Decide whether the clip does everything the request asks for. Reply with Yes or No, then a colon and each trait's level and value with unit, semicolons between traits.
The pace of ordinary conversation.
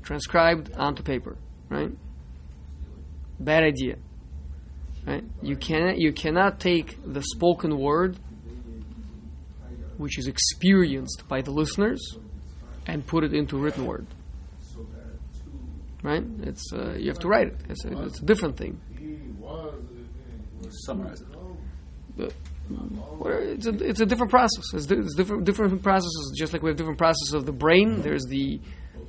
No: slow, 130 wpm